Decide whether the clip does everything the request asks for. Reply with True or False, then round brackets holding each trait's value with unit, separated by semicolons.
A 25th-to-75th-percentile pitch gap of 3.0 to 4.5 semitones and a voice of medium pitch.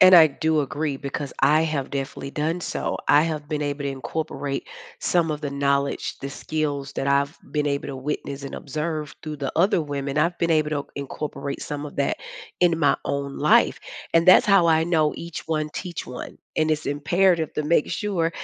False (2.4 semitones; 150 Hz)